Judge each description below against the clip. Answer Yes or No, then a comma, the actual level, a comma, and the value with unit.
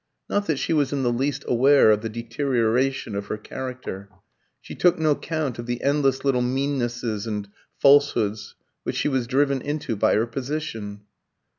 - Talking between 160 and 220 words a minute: Yes, average, 170 wpm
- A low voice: Yes, low, 130 Hz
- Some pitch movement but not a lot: Yes, average, 3.8 semitones